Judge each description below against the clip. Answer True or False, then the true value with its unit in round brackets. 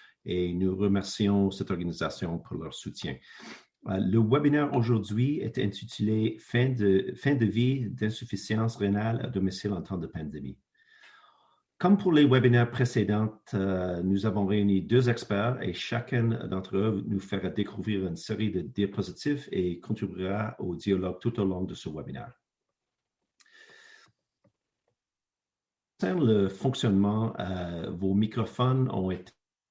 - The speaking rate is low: True (135 wpm)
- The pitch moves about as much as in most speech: True (3.8 semitones)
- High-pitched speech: False (105 Hz)